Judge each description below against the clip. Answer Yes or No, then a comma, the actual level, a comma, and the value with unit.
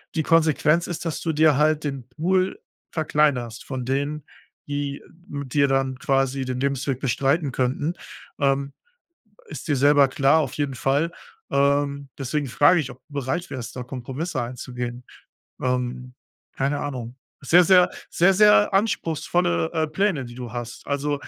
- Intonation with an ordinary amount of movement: Yes, average, 3.3 semitones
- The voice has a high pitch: No, medium, 140 Hz